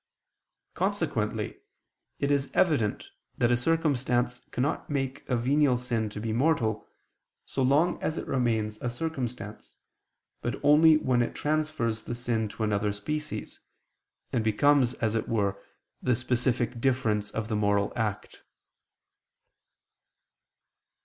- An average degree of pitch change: Yes, average, 4.3 semitones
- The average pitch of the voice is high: No, low, 120 Hz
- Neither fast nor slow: No, slow, 125 wpm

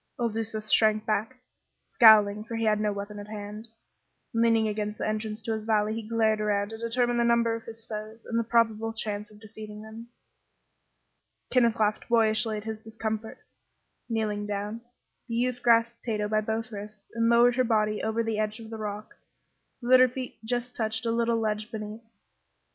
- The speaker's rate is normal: Yes, average, 185 wpm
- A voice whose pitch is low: No, high, 220 Hz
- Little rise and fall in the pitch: Yes, narrow, 1.4 semitones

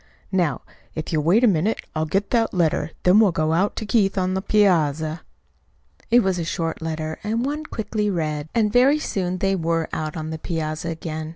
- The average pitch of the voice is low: No, medium, 175 Hz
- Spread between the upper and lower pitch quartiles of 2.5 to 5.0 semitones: Yes, average, 4.7 semitones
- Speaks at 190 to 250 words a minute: Yes, average, 200 wpm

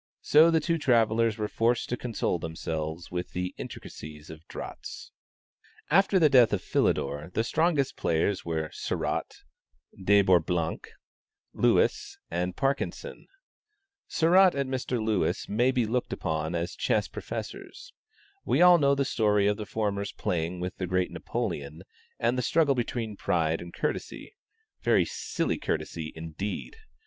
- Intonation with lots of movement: Yes, wide, 7.4 semitones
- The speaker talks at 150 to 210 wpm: No, average, 140 wpm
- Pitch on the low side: Yes, low, 105 Hz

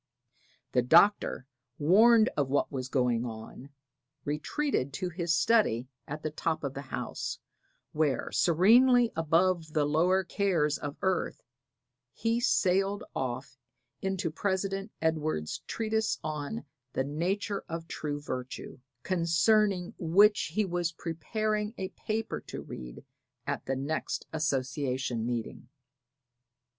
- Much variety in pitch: Yes, wide, 5.8 semitones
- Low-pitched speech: No, medium, 165 Hz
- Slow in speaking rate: Yes, slow, 120 wpm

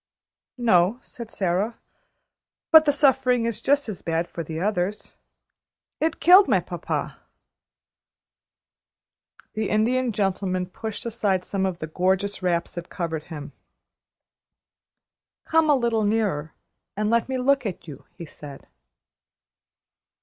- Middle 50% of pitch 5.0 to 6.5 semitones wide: Yes, average, 5.3 semitones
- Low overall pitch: No, high, 205 Hz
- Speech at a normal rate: No, slow, 125 wpm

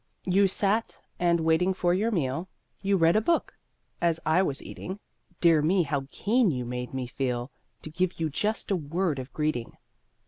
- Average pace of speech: Yes, average, 180 wpm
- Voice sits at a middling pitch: Yes, medium, 170 Hz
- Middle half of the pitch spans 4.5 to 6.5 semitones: Yes, average, 5.1 semitones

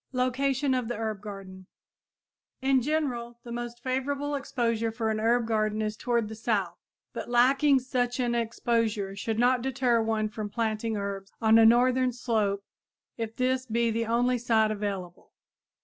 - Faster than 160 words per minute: No, average, 155 wpm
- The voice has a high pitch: Yes, high, 235 Hz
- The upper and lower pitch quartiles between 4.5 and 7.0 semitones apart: No, narrow, 2.6 semitones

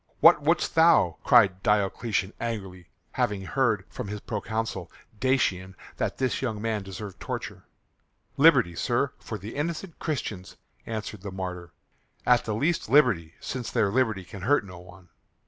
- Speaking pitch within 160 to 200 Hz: No, low, 110 Hz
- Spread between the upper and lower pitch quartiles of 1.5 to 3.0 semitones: No, average, 5.1 semitones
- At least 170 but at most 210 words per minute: No, average, 145 wpm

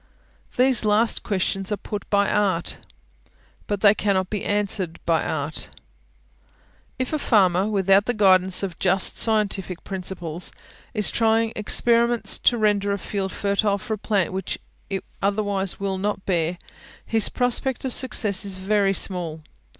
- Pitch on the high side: Yes, high, 200 Hz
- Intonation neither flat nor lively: No, narrow, 2.2 semitones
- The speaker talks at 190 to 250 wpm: No, average, 145 wpm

